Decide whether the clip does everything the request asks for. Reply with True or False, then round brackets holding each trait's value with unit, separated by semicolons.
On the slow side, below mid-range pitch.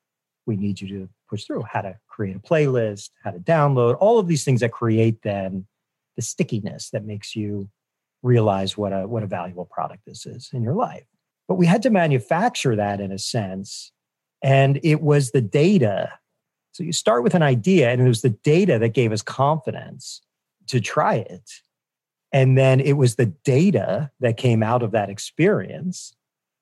False (185 wpm; 125 Hz)